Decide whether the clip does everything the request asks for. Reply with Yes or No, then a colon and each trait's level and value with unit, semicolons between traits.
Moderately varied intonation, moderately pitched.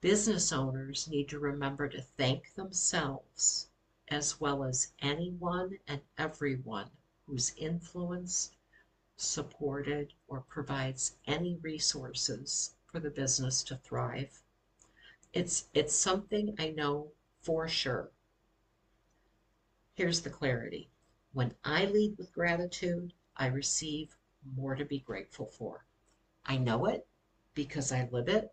Yes: average, 4.0 semitones; medium, 145 Hz